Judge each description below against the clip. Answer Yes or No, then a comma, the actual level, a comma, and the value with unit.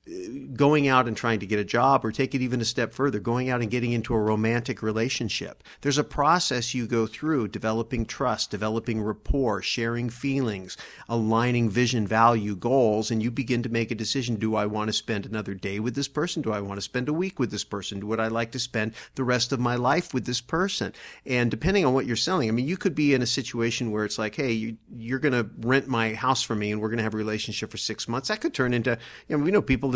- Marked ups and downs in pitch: No, average, 3.1 semitones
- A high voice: No, low, 120 Hz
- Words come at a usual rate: No, fast, 250 wpm